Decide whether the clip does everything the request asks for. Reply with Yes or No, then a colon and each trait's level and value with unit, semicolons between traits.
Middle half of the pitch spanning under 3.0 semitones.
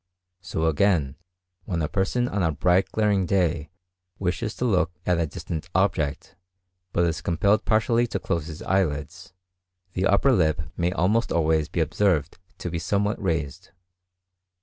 No: average, 3.7 semitones